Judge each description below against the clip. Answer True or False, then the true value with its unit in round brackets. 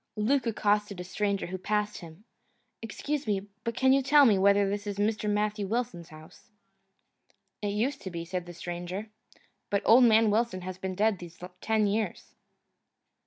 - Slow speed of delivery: False (170 wpm)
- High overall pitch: True (205 Hz)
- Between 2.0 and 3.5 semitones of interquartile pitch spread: True (2.9 semitones)